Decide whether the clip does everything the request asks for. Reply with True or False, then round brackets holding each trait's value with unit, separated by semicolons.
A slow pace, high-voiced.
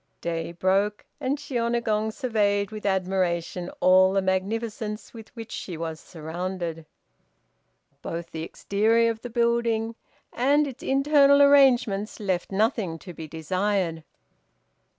True (120 wpm; 205 Hz)